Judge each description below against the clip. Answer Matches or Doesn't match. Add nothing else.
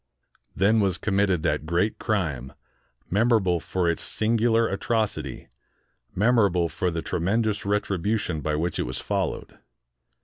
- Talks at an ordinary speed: Doesn't match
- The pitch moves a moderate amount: Matches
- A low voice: Matches